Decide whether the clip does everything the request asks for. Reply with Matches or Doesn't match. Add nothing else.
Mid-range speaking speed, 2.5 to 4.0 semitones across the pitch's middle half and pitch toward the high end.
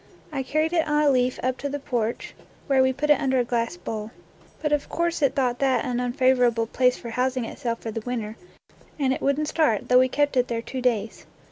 Doesn't match